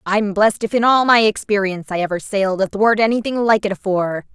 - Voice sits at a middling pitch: No, high, 205 Hz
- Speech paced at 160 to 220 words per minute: Yes, fast, 205 wpm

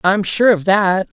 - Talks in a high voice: Yes, high, 195 Hz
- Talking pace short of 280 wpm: Yes, fast, 205 wpm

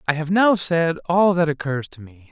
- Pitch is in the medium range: Yes, medium, 160 Hz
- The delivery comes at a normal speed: No, fast, 235 wpm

